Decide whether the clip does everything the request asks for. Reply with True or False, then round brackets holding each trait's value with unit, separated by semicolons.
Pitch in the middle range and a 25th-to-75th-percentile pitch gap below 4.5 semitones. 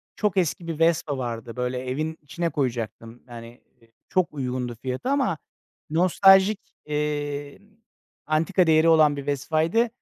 False (150 Hz; 4.8 semitones)